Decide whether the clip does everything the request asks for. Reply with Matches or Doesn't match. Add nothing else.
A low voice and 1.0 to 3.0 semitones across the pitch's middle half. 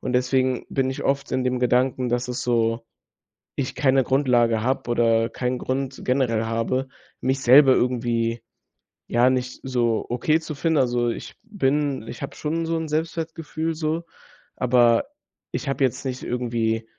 Matches